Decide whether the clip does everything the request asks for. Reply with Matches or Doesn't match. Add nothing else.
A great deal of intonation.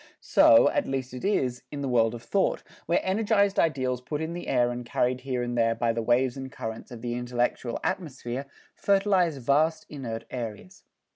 Doesn't match